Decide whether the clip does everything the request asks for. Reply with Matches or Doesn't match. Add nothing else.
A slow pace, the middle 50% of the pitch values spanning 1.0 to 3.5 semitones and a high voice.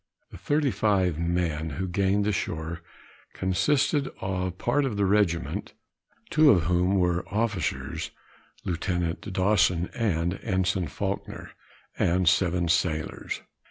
Doesn't match